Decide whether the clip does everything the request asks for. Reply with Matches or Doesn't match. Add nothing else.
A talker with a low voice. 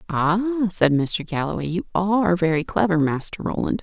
Doesn't match